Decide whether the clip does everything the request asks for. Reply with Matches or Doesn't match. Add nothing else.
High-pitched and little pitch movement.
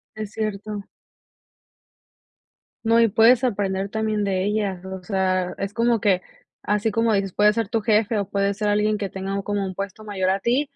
Matches